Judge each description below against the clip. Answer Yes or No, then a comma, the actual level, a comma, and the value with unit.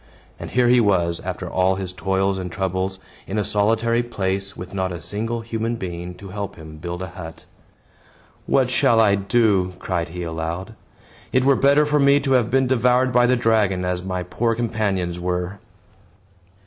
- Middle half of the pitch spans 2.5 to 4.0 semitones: No, average, 4.4 semitones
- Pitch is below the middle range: Yes, low, 100 Hz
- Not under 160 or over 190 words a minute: Yes, average, 180 wpm